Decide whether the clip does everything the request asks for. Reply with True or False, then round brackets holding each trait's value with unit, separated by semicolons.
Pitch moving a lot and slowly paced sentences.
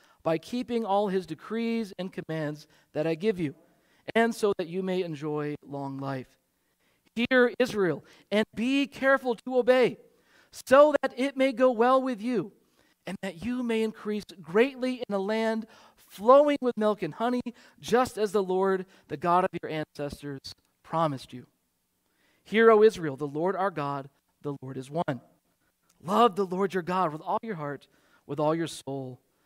False (7.1 semitones; 170 wpm)